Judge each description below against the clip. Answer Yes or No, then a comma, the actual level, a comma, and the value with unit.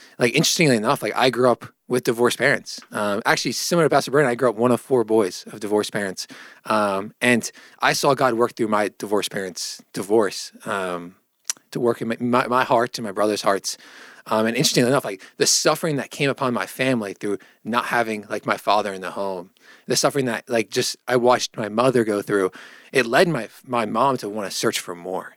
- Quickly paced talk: Yes, fast, 220 wpm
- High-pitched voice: No, low, 120 Hz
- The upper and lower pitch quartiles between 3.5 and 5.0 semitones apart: No, average, 2.9 semitones